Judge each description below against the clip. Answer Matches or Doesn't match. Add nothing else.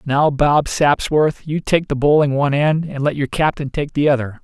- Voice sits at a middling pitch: Matches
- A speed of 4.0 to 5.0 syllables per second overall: Matches